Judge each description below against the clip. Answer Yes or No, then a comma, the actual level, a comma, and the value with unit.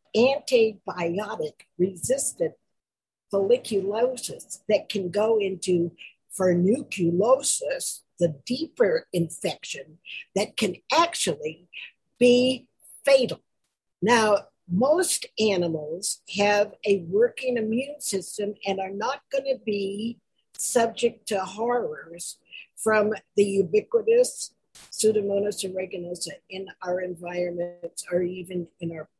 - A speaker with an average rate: No, slow, 90 wpm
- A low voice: No, high, 205 Hz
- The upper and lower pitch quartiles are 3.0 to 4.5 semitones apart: No, average, 5.2 semitones